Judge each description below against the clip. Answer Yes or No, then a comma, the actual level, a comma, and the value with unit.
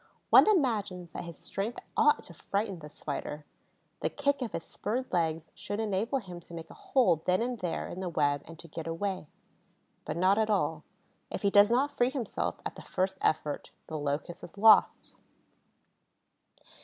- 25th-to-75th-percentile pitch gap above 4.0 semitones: Yes, average, 5.2 semitones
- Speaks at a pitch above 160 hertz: Yes, high, 190 Hz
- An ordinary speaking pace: Yes, average, 180 wpm